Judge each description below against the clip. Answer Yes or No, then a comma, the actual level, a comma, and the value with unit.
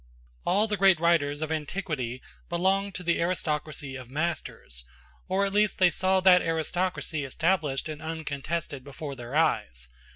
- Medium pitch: Yes, medium, 160 Hz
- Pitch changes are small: No, average, 4.4 semitones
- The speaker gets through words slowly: No, average, 150 wpm